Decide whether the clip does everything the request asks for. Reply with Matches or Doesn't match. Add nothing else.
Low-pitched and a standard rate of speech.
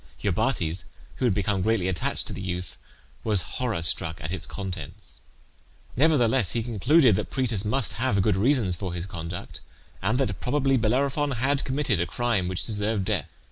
Matches